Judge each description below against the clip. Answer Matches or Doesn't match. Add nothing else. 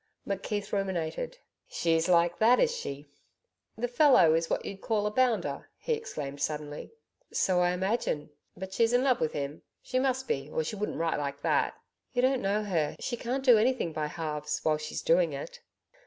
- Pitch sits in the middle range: Doesn't match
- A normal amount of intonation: Doesn't match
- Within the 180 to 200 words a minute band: Matches